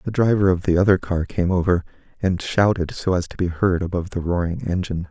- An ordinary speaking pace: No, fast, 225 wpm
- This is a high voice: No, very low, 90 Hz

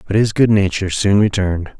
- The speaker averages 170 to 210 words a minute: Yes, average, 200 wpm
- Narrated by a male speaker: Yes, male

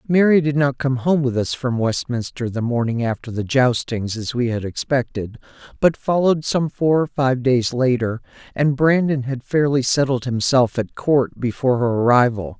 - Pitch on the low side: Yes, low, 130 Hz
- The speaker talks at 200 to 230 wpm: No, average, 175 wpm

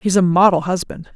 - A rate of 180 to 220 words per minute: Yes, fast, 205 wpm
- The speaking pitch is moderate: Yes, medium, 180 Hz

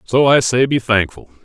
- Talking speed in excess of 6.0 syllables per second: No, 5.0 syllables/s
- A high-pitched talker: No, low, 115 Hz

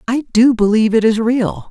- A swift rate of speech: Yes, fast, 210 wpm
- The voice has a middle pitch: No, high, 225 Hz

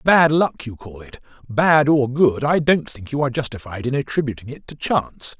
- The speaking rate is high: Yes, fast, 210 wpm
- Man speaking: Yes, male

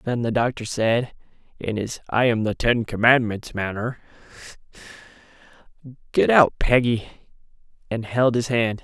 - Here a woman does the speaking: No, male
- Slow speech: Yes, slow, 130 wpm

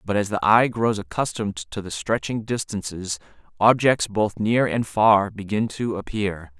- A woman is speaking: No, male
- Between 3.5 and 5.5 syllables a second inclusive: Yes, 4.5 syllables/s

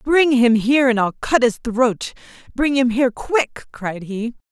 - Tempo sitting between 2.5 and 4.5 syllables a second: Yes, 4.4 syllables/s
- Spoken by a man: No, female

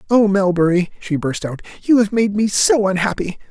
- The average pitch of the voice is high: Yes, high, 195 Hz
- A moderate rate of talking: Yes, average, 190 wpm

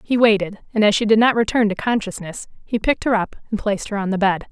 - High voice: Yes, high, 210 Hz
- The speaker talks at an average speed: No, fast, 265 wpm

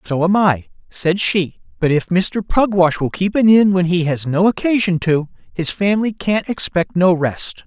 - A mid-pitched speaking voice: Yes, medium, 180 Hz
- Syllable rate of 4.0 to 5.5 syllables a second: Yes, 4.5 syllables/s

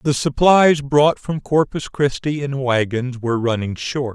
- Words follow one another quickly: No, average, 160 wpm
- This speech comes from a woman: No, male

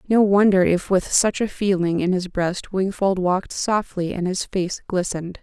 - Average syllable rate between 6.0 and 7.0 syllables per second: No, 4.6 syllables/s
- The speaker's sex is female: Yes, female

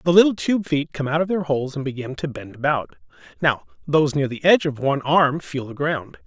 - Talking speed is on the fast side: Yes, fast, 240 wpm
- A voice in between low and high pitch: Yes, medium, 145 Hz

